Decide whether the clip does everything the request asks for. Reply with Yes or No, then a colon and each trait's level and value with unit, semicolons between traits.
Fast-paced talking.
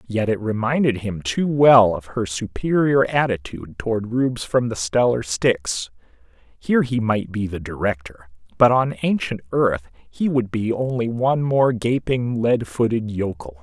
No: average, 160 wpm